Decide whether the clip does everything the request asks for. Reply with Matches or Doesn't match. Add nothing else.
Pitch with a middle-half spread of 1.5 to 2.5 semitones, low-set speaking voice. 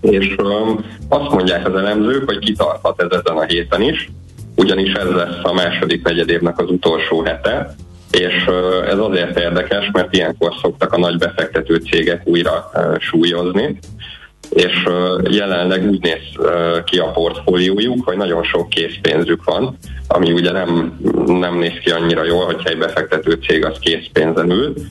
Matches